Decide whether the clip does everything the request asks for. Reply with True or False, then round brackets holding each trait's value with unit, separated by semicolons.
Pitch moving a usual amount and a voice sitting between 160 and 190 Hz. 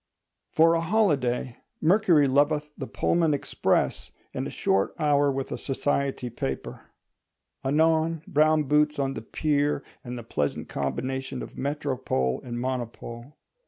False (3.5 semitones; 140 Hz)